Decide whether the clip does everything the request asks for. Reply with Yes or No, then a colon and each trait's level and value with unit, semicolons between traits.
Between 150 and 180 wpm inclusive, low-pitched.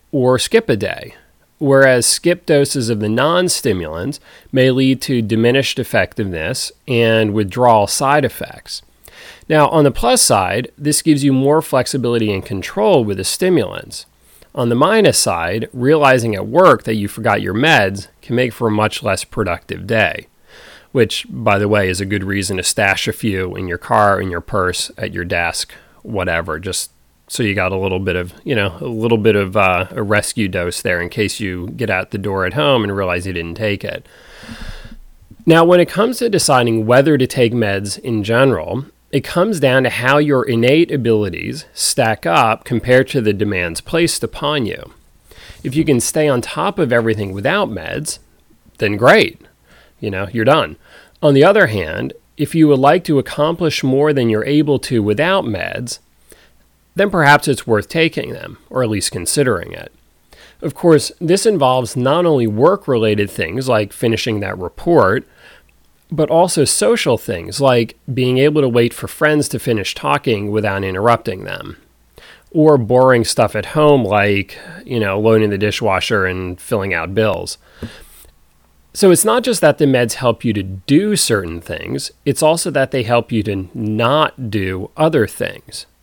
Yes: average, 175 wpm; low, 115 Hz